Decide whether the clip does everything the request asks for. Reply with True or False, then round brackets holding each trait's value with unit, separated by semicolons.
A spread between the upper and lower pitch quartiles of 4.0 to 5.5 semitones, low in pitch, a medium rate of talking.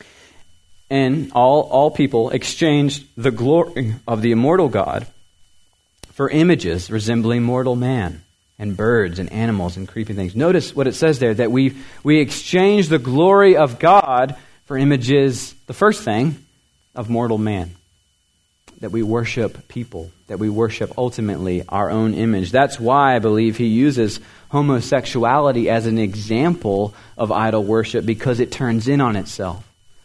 True (4.4 semitones; 115 Hz; 150 wpm)